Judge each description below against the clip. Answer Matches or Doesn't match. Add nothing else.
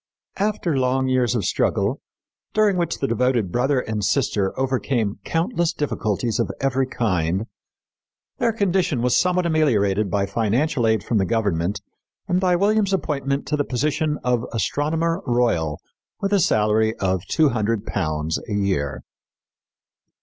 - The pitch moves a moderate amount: Doesn't match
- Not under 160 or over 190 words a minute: Doesn't match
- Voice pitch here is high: Doesn't match